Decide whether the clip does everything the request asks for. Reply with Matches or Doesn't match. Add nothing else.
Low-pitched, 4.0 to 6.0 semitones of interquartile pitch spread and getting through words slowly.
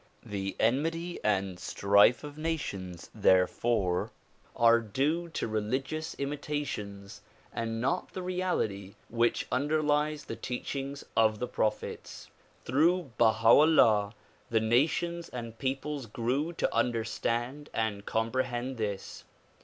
Matches